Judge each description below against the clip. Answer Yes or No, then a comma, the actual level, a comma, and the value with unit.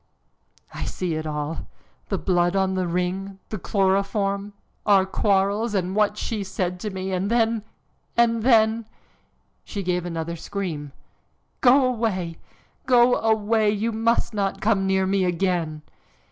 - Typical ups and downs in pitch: Yes, average, 3.3 semitones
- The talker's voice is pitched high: Yes, high, 195 Hz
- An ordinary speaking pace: Yes, average, 145 wpm